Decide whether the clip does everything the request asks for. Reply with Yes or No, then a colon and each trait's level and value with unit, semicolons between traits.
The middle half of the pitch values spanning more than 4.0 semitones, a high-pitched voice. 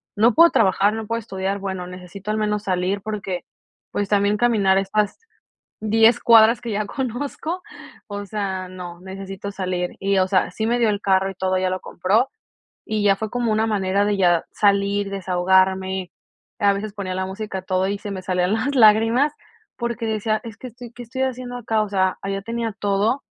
No: average, 2.8 semitones; high, 200 Hz